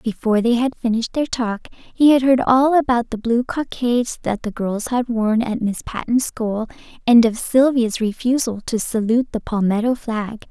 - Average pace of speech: Yes, average, 185 wpm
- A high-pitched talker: Yes, high, 235 Hz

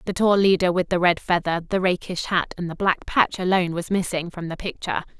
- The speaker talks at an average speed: No, fast, 230 wpm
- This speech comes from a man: No, female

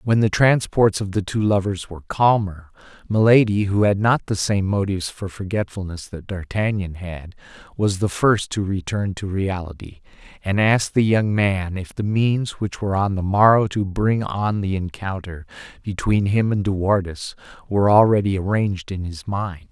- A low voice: Yes, low, 100 Hz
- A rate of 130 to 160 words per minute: No, average, 175 wpm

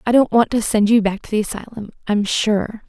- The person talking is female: Yes, female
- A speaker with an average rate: No, fast, 250 wpm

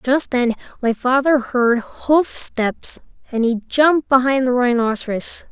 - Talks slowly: Yes, slow, 130 wpm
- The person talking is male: No, female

